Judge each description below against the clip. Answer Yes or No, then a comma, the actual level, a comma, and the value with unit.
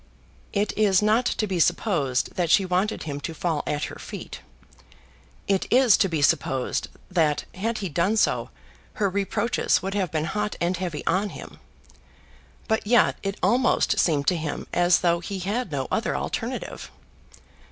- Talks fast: No, average, 165 wpm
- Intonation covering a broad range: No, average, 4.2 semitones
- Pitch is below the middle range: No, medium, 185 Hz